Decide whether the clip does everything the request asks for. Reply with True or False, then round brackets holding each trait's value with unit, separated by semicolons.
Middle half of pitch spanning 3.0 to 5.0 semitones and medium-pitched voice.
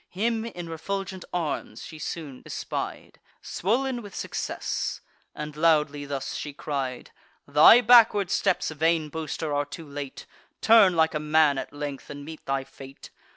True (4.5 semitones; 155 Hz)